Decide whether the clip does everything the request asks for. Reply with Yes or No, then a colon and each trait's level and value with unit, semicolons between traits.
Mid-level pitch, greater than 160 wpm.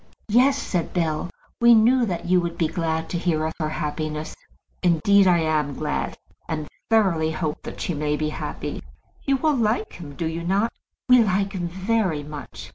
Yes: medium, 170 Hz; average, 185 wpm